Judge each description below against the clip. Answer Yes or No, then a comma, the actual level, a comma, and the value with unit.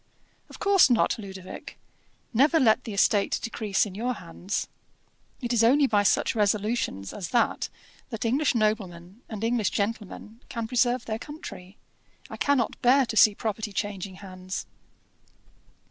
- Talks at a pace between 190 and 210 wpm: No, average, 145 wpm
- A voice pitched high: Yes, high, 220 Hz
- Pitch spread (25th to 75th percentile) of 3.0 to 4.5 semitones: Yes, average, 3.4 semitones